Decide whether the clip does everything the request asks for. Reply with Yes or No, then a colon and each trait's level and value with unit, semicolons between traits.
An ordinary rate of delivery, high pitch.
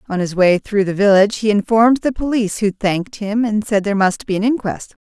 No: fast, 235 wpm; high, 210 Hz